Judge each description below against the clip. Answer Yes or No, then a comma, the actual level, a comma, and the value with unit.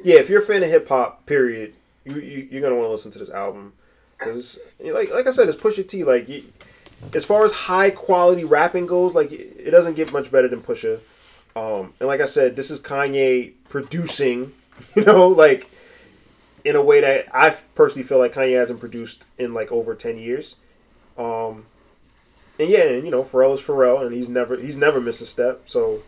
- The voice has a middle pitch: Yes, medium, 180 Hz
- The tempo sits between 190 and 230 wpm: Yes, fast, 205 wpm